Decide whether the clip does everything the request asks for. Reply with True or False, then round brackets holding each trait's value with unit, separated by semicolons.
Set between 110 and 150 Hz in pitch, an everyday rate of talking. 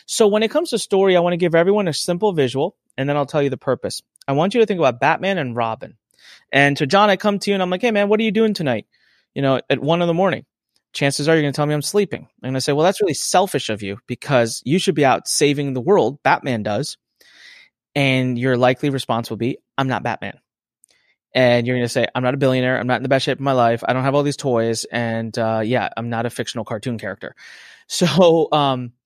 False (140 Hz; 265 wpm)